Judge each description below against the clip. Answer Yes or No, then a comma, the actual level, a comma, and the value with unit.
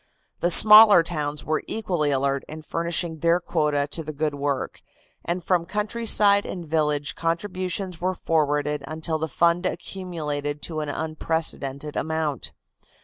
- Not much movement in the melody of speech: No, average, 3.0 semitones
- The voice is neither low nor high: Yes, medium, 160 Hz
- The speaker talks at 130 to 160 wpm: Yes, average, 140 wpm